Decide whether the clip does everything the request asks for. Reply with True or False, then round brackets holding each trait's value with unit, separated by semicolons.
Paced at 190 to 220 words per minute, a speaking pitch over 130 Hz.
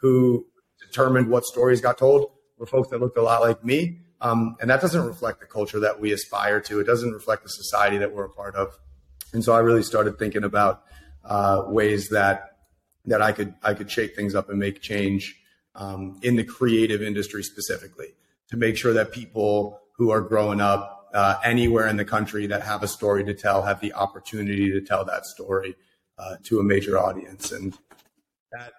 False (200 wpm; 105 Hz)